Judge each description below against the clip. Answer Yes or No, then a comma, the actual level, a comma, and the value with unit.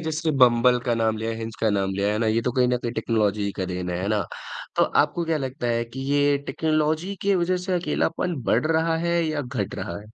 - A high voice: No, low, 125 Hz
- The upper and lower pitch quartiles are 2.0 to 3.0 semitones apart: No, wide, 6.3 semitones